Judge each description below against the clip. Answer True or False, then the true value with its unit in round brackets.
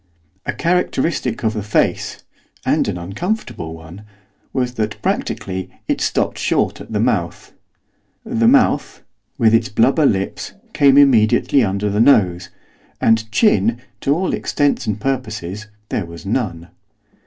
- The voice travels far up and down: True (6.3 semitones)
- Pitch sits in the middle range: False (110 Hz)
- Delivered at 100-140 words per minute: True (135 wpm)